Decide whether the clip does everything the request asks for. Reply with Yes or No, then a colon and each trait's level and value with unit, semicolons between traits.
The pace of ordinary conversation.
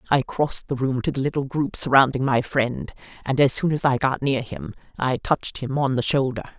No: fast, 230 wpm